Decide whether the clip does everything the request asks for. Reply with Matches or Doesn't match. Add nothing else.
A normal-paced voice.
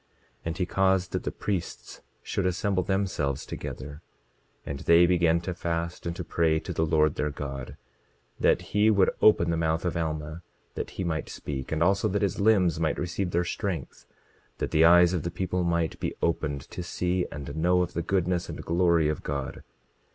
Matches